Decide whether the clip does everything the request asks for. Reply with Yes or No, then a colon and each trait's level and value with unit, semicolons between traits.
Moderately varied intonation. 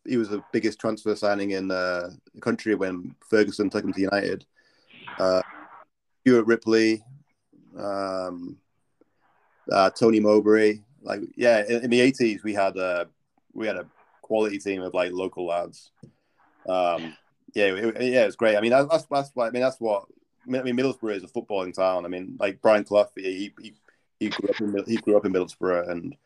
Yes: average, 3.5 semitones